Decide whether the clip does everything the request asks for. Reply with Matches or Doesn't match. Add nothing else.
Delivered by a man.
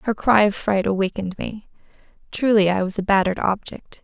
Doesn't match